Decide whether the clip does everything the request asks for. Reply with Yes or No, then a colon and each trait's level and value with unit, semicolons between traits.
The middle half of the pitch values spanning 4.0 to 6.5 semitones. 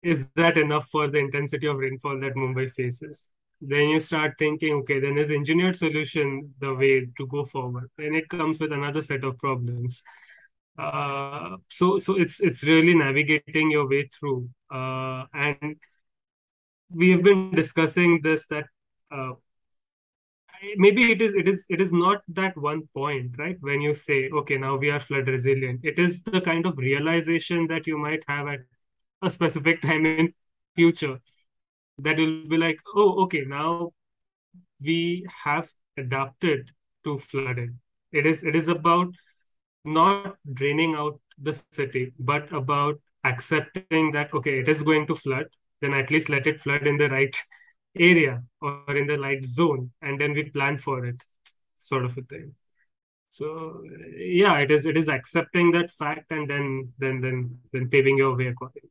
No: average, 3.1 semitones